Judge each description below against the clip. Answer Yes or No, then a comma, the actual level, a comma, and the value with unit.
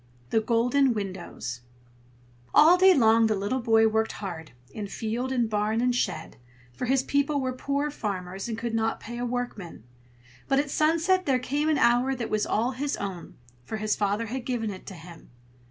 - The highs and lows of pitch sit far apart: No, average, 4.0 semitones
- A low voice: No, high, 235 Hz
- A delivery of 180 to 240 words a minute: Yes, average, 185 wpm